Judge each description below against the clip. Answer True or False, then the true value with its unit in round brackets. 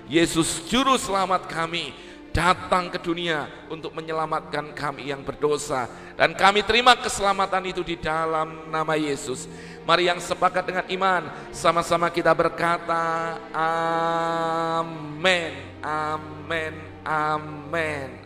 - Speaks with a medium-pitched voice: True (165 Hz)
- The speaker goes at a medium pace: True (105 wpm)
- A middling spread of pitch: False (2.3 semitones)